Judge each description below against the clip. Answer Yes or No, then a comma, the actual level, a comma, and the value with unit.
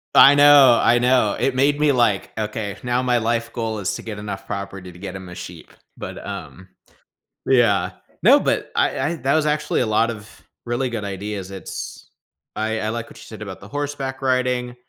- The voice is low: Yes, low, 115 Hz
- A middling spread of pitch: Yes, average, 4.0 semitones